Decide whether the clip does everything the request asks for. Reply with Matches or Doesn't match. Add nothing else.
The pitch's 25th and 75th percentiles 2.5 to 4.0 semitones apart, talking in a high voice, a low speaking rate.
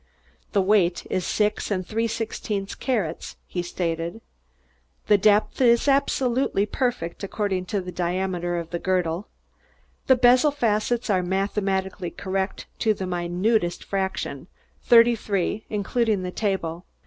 Matches